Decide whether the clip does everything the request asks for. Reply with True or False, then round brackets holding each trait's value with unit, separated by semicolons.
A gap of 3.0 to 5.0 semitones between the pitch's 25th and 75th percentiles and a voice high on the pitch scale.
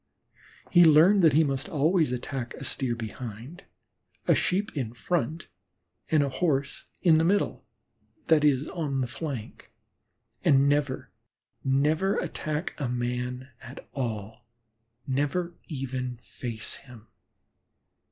False (4.2 semitones; 140 Hz)